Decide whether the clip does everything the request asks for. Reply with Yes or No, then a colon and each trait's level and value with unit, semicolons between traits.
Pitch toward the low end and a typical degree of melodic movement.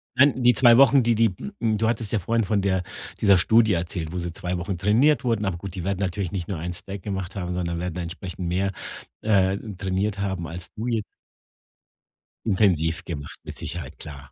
Yes: very low, 95 Hz; average, 3.8 semitones